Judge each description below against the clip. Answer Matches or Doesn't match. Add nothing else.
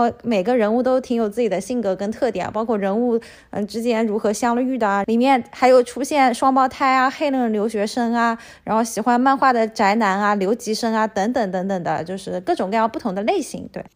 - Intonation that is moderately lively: Matches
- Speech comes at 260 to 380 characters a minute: Matches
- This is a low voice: Doesn't match